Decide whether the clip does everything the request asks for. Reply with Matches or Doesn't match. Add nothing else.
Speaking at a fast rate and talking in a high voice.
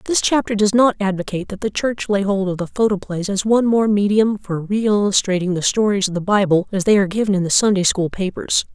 Matches